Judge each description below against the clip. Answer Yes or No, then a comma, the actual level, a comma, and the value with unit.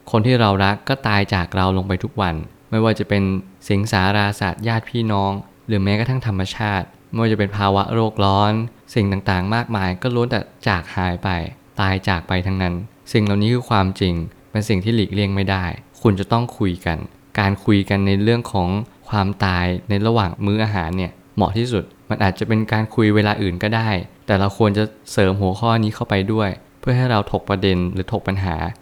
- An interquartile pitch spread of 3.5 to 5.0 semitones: No, average, 2.8 semitones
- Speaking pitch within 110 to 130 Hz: No, low, 100 Hz